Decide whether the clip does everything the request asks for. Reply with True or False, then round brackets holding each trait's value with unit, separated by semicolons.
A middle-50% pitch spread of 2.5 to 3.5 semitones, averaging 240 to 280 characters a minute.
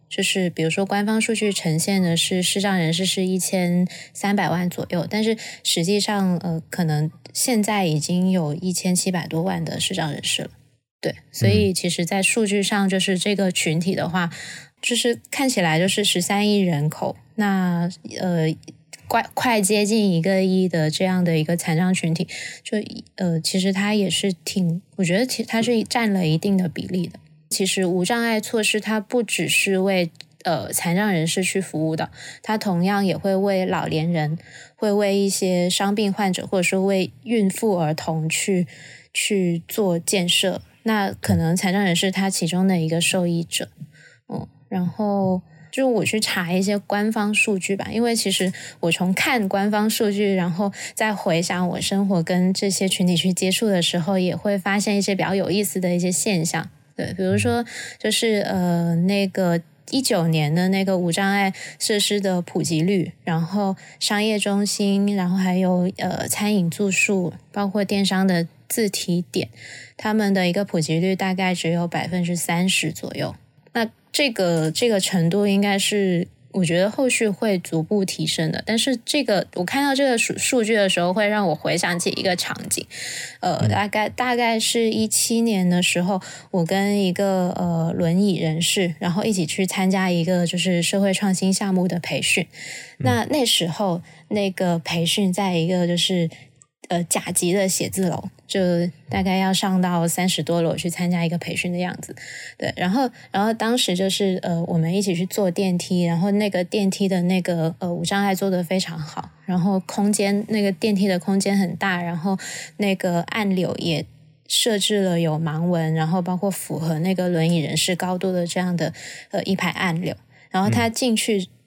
True (2.8 semitones; 260 characters per minute)